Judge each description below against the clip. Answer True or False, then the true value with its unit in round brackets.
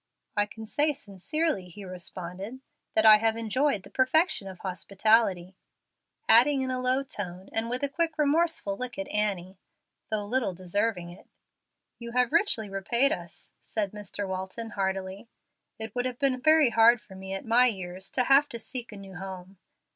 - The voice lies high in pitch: True (220 Hz)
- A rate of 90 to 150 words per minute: False (175 wpm)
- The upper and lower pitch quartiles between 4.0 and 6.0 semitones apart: True (4.8 semitones)